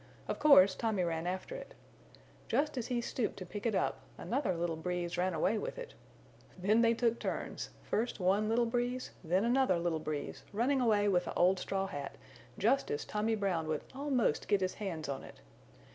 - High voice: Yes, high, 205 Hz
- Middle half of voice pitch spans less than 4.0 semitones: No, average, 5.0 semitones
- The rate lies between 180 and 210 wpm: Yes, average, 190 wpm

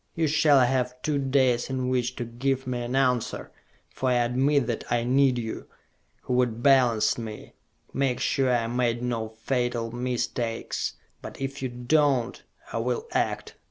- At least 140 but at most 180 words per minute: Yes, average, 165 wpm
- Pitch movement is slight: Yes, narrow, 1.9 semitones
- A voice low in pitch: Yes, low, 125 Hz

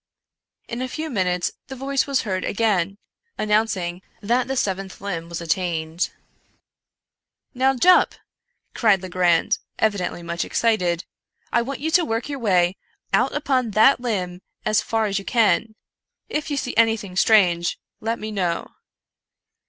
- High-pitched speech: Yes, high, 215 Hz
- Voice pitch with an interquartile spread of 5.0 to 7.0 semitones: Yes, average, 5.3 semitones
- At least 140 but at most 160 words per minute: Yes, average, 150 wpm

